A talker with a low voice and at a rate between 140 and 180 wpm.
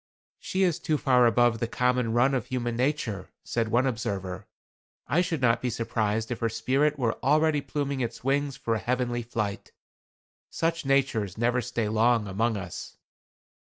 Yes: low, 120 Hz; average, 165 wpm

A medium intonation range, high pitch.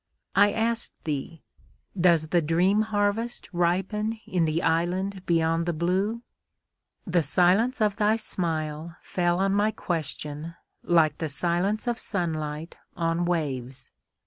No: average, 3.9 semitones; medium, 175 Hz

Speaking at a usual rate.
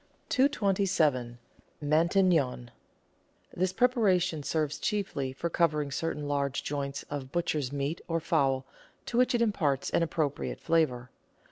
No: slow, 125 wpm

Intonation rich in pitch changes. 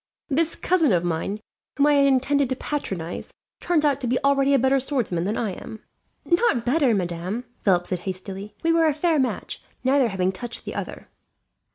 Yes: wide, 6.8 semitones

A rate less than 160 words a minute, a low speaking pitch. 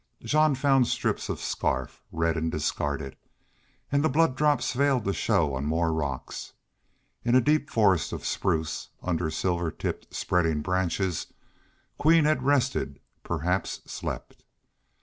Yes: slow, 135 wpm; very low, 95 Hz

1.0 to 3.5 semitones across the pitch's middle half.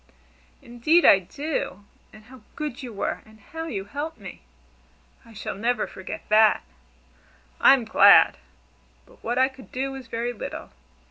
No: average, 3.9 semitones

